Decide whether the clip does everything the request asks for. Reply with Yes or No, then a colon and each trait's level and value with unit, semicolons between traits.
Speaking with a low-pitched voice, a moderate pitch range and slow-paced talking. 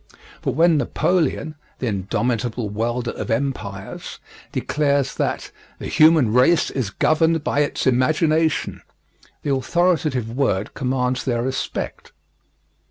Yes: low, 130 Hz; average, 4.6 semitones; slow, 110 wpm